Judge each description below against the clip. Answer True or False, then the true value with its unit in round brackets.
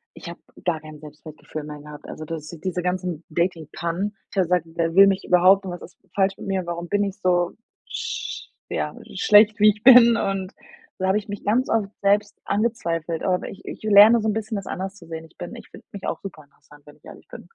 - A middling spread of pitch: True (3.5 semitones)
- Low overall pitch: False (185 Hz)